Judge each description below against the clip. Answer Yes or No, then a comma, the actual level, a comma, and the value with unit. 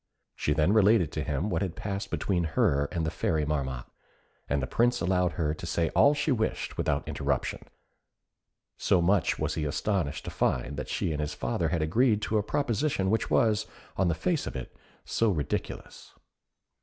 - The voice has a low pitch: Yes, very low, 85 Hz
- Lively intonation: Yes, wide, 5.9 semitones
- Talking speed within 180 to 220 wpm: Yes, average, 185 wpm